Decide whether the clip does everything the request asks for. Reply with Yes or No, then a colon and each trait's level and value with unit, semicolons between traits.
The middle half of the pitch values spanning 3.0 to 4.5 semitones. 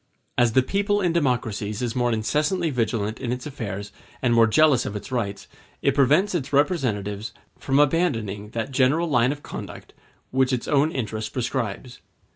No: average, 4.9 semitones